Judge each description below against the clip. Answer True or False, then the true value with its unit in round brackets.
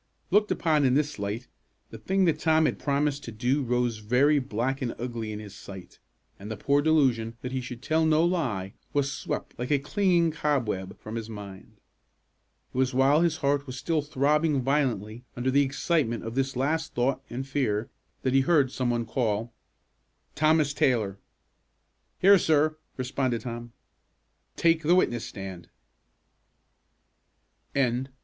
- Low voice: True (130 Hz)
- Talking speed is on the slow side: False (155 wpm)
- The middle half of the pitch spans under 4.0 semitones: False (4.5 semitones)